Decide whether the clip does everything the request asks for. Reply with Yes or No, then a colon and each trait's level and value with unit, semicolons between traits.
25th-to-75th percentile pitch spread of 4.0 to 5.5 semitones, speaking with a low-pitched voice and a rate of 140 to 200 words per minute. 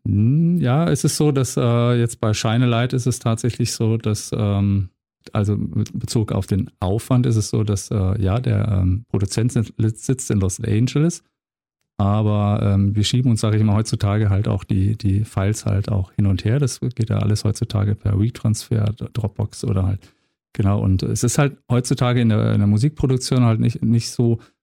No: average, 2.7 semitones; low, 110 Hz; fast, 190 wpm